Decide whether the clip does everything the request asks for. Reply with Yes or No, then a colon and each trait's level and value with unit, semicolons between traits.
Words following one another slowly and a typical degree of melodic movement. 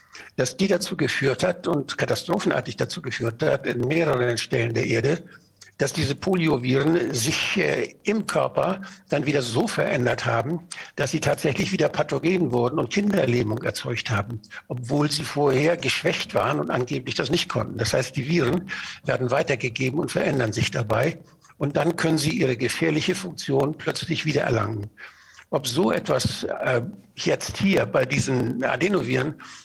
No: average, 155 wpm; average, 5.0 semitones